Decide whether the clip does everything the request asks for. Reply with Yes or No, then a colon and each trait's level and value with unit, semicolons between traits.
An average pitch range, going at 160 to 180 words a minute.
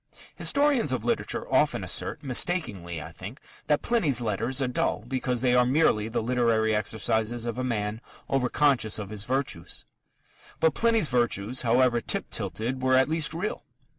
Yes: average, 3.6 semitones; average, 165 wpm